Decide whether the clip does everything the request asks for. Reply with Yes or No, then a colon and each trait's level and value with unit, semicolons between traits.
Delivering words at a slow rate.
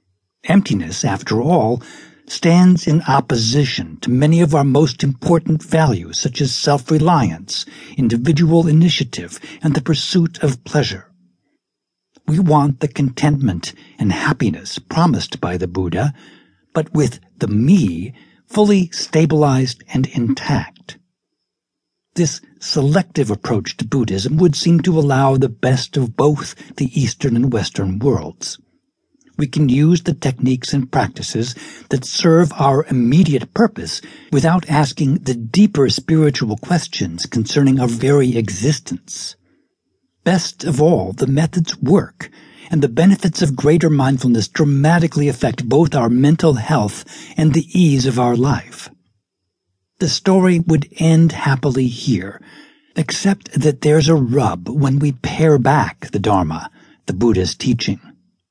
Yes: slow, 130 wpm